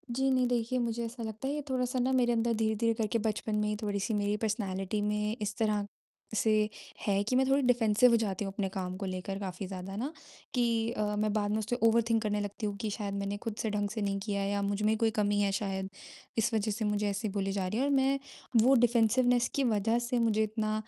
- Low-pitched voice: No, high, 215 Hz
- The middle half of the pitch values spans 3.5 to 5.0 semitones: No, narrow, 2.5 semitones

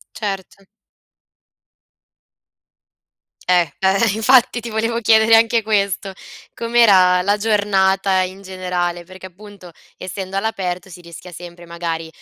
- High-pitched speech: Yes, high, 195 Hz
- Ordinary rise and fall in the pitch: Yes, average, 3.3 semitones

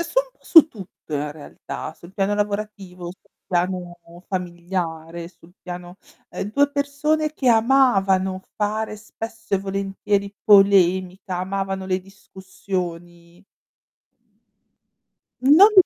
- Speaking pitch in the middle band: No, high, 195 Hz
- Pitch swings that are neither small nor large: Yes, average, 3.3 semitones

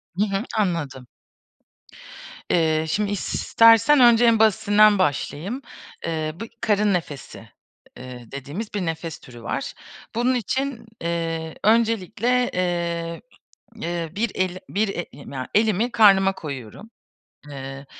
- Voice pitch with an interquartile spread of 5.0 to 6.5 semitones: Yes, wide, 5.6 semitones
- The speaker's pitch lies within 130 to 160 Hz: No, medium, 185 Hz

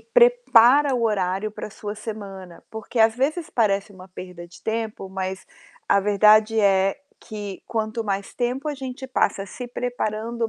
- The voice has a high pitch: Yes, high, 215 Hz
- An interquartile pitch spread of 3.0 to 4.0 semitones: Yes, average, 3.5 semitones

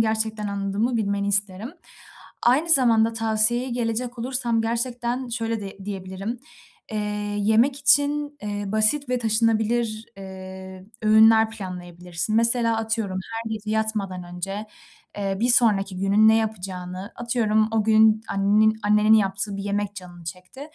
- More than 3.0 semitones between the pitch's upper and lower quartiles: No, average, 2.7 semitones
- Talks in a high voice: Yes, high, 220 Hz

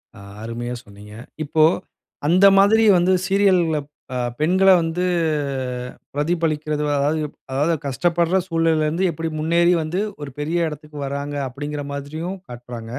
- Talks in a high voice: No, medium, 155 Hz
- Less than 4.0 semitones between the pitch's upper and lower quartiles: Yes, average, 3.3 semitones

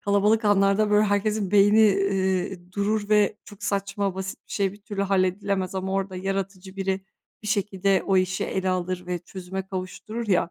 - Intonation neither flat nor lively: No, narrow, 1.5 semitones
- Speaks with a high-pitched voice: Yes, high, 195 Hz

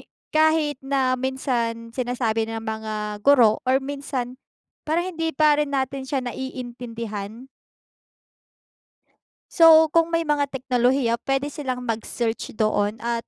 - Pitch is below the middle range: No, very high, 255 Hz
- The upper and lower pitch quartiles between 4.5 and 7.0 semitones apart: No, average, 3.7 semitones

